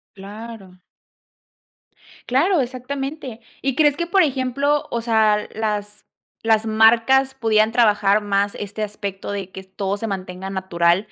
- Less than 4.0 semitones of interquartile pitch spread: No, average, 4.4 semitones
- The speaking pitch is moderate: No, high, 220 Hz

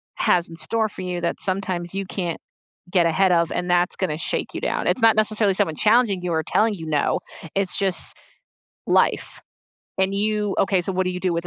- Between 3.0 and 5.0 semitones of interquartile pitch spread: No, narrow, 2.5 semitones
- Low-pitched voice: No, medium, 185 Hz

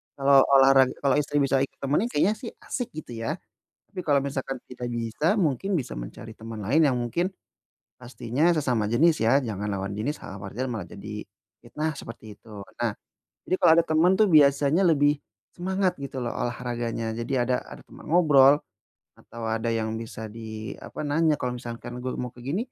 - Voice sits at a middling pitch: No, low, 130 Hz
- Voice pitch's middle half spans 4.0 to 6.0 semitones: Yes, average, 4.4 semitones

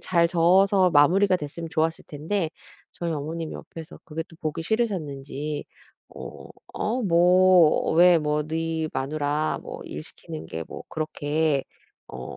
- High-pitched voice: No, medium, 160 Hz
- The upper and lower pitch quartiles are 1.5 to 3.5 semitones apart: Yes, average, 2.9 semitones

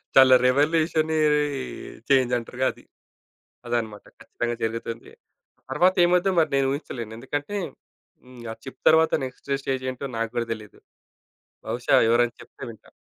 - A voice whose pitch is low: Yes, low, 130 Hz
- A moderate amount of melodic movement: Yes, average, 3.6 semitones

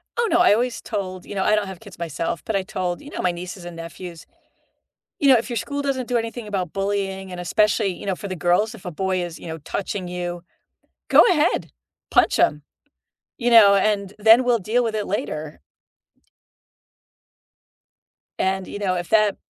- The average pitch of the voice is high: Yes, high, 195 Hz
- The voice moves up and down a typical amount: Yes, average, 3.8 semitones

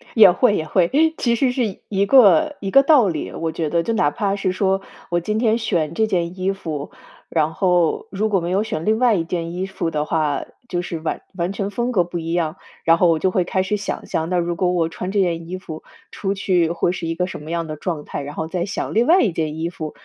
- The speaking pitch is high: No, medium, 180 Hz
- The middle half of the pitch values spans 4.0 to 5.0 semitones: No, average, 3.5 semitones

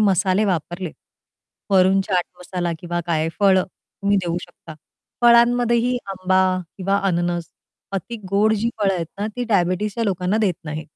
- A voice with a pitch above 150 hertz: Yes, high, 190 Hz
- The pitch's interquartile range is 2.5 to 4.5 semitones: Yes, average, 2.9 semitones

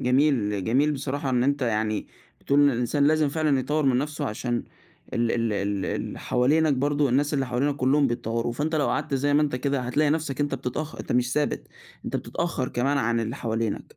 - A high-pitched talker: No, low, 135 Hz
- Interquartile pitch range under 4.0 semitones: Yes, average, 3.3 semitones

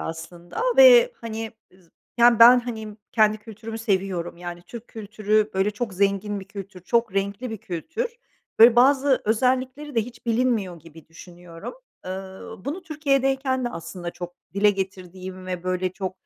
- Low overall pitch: No, high, 210 Hz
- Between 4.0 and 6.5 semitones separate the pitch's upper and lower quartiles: Yes, average, 4.7 semitones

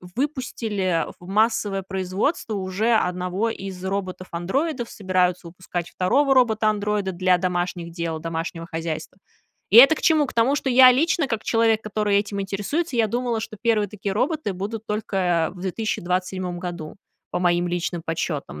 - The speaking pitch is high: Yes, high, 195 Hz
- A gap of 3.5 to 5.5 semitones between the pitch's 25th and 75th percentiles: Yes, average, 4.1 semitones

